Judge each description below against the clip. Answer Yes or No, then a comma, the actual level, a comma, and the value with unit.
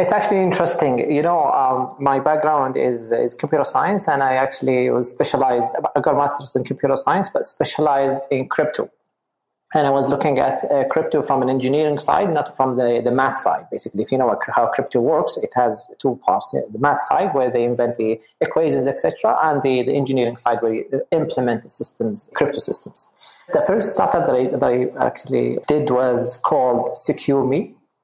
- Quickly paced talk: No, average, 190 wpm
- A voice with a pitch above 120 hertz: Yes, low, 135 Hz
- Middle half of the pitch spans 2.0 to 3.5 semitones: Yes, average, 2.9 semitones